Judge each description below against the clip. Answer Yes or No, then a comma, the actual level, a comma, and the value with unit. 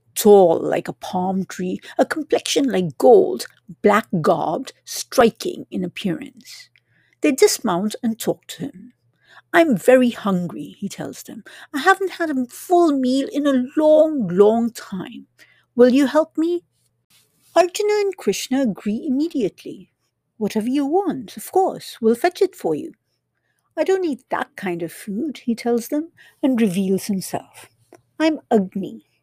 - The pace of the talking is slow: No, average, 150 wpm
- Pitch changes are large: Yes, wide, 7.6 semitones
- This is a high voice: Yes, high, 245 Hz